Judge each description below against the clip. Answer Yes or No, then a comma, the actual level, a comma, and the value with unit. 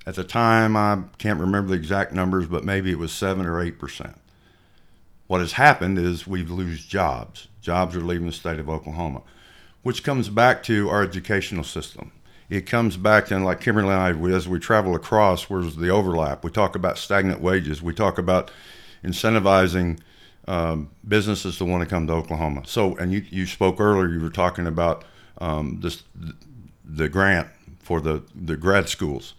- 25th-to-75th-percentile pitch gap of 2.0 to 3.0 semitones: Yes, average, 2.7 semitones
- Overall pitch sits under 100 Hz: Yes, very low, 90 Hz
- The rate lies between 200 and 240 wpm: No, average, 180 wpm